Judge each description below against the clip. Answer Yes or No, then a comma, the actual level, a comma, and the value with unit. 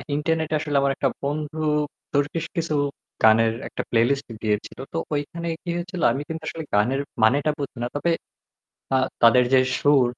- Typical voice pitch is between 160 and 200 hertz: No, medium, 145 Hz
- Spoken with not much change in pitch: No, average, 4.1 semitones